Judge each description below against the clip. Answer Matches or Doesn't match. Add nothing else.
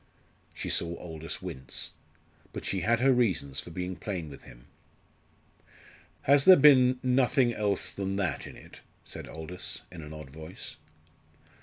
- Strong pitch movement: Matches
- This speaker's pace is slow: Doesn't match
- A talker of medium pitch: Doesn't match